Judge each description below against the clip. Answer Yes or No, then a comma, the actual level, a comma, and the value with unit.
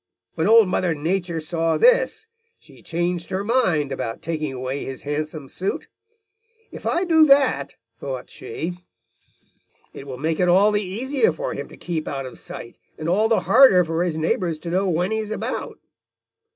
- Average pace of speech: Yes, average, 180 wpm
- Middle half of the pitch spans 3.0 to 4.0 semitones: No, average, 5.2 semitones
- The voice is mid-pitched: Yes, medium, 175 Hz